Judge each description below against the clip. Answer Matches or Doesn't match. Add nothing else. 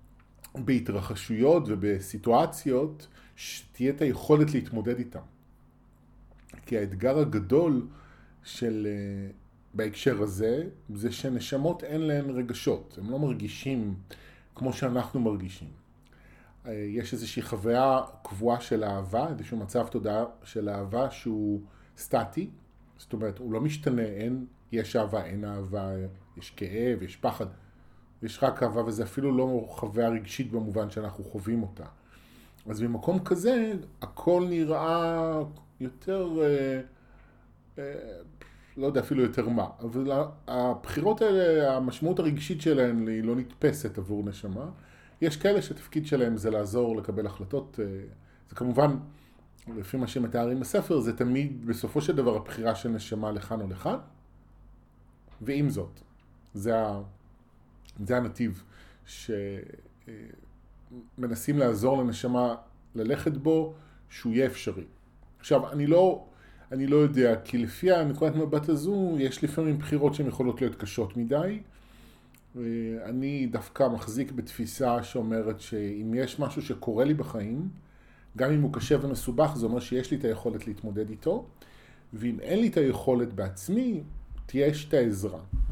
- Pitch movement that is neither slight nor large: Matches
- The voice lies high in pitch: Doesn't match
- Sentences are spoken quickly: Doesn't match